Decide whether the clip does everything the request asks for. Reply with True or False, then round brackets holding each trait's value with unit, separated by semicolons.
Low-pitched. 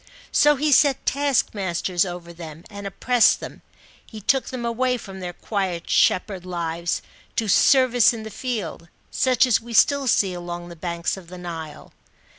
False (195 Hz)